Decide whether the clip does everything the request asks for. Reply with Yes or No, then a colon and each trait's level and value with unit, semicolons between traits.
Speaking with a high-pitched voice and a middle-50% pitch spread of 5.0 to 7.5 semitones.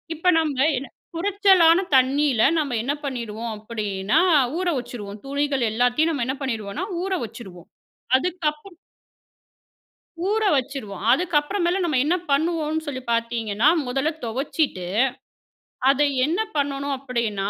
Yes: very high, 275 Hz; wide, 5.4 semitones